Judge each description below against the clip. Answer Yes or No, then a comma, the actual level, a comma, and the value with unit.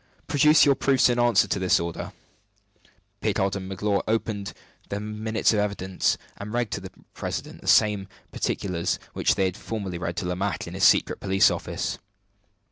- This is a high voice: No, low, 100 Hz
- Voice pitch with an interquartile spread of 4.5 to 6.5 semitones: No, average, 2.7 semitones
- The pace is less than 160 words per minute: No, average, 170 wpm